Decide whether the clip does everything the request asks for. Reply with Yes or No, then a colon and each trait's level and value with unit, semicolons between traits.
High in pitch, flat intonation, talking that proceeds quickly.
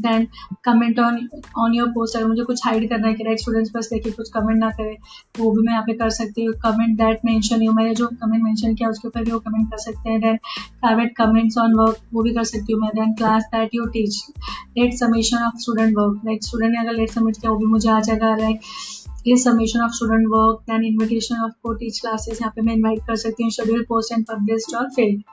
No: high, 225 Hz; narrow, 0.7 semitones; average, 115 wpm